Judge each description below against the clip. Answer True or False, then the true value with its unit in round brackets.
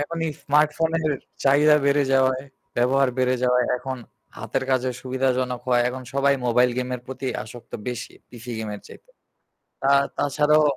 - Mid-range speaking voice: False (130 Hz)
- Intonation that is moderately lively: False (2.3 semitones)